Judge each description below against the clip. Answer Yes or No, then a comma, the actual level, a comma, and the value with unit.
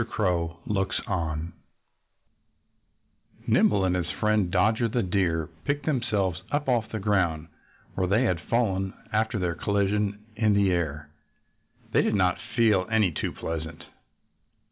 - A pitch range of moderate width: Yes, average, 3.9 semitones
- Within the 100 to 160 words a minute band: Yes, slow, 135 wpm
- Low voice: Yes, very low, 95 Hz